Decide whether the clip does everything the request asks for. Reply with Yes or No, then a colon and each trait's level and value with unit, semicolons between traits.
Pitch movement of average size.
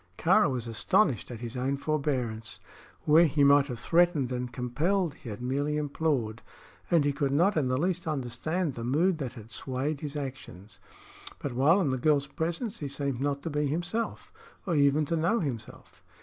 Yes: average, 4.1 semitones